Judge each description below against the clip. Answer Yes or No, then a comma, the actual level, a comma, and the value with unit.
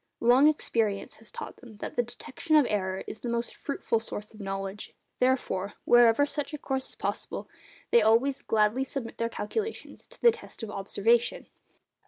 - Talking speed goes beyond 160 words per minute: Yes, average, 175 wpm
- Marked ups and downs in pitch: No, average, 3.9 semitones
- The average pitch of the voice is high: Yes, high, 235 Hz